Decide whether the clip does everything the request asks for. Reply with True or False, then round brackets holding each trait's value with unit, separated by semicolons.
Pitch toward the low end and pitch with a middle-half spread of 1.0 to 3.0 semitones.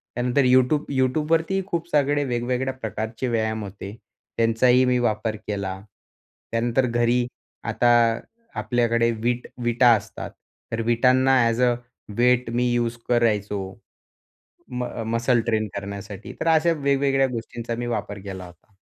True (120 Hz; 2.5 semitones)